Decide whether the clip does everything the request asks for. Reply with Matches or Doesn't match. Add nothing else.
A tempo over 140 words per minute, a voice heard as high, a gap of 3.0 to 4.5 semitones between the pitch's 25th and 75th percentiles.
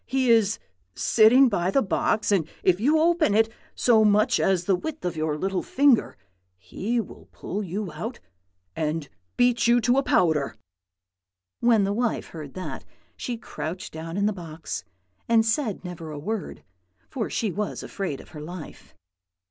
Doesn't match